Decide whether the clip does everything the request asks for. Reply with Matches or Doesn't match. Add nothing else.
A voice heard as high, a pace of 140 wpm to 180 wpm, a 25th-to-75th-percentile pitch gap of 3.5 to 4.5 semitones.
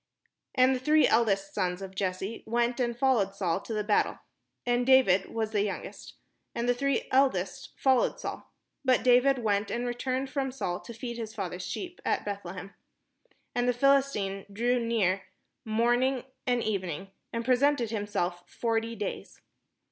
Matches